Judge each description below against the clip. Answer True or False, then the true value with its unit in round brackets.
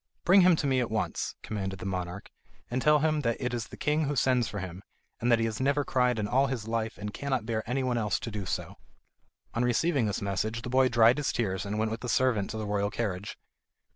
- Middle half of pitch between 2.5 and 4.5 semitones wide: True (3.8 semitones)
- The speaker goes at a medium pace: False (245 wpm)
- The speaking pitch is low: True (115 Hz)